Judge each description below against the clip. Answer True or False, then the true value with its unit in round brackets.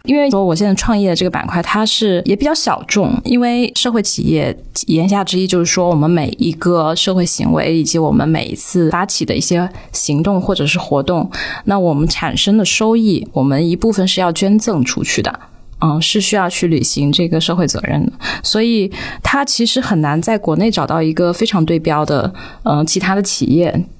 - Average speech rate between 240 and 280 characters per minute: False (300 characters per minute)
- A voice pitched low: False (180 Hz)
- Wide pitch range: False (4.4 semitones)